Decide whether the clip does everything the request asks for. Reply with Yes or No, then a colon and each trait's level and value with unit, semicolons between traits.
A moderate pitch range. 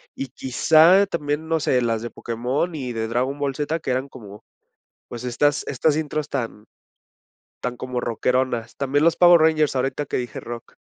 Yes: average, 3.8 semitones